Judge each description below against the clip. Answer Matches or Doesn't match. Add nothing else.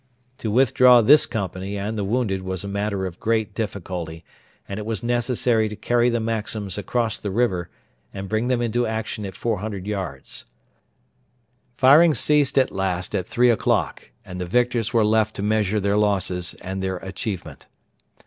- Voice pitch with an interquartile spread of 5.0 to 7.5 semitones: Doesn't match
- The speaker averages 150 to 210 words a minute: Matches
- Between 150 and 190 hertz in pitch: Doesn't match